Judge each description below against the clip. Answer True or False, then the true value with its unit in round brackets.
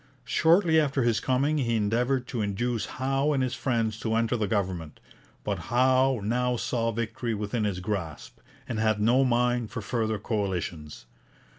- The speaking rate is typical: True (160 wpm)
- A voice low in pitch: True (115 Hz)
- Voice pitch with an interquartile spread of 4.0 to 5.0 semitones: False (3.3 semitones)